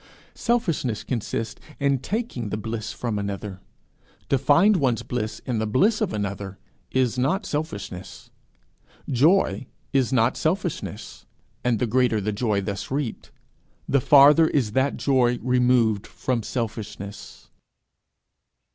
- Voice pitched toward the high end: No, low, 125 Hz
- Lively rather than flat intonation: No, average, 4.5 semitones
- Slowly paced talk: Yes, slow, 125 wpm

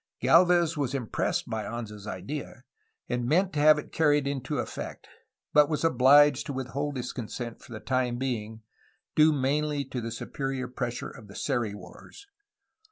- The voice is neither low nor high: No, low, 130 Hz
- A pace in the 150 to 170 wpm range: Yes, average, 165 wpm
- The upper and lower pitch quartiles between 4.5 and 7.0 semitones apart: No, average, 3.5 semitones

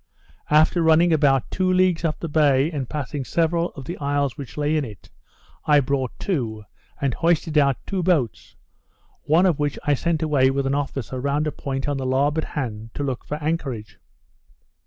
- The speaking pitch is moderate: Yes, medium, 145 Hz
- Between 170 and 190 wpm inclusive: Yes, average, 185 wpm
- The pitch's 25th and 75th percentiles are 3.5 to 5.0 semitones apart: No, average, 3.1 semitones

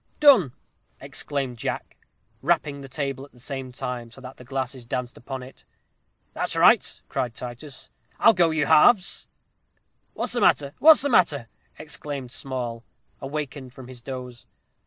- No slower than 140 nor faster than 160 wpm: Yes, average, 150 wpm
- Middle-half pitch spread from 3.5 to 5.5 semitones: No, average, 3.0 semitones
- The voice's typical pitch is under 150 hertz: Yes, low, 135 Hz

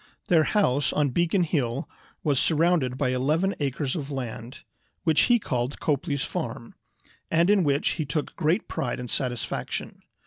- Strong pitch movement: No, average, 4.3 semitones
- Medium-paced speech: Yes, average, 150 wpm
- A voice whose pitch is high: No, medium, 145 Hz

